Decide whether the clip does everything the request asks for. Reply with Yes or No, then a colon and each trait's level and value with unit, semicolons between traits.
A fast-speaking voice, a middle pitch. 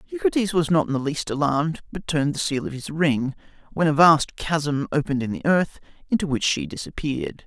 Yes: fast, 210 wpm; medium, 150 Hz